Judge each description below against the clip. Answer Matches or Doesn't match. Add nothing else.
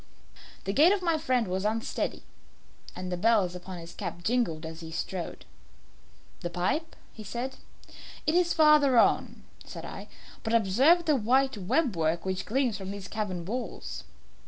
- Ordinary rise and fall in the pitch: Doesn't match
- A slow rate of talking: Doesn't match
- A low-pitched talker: Doesn't match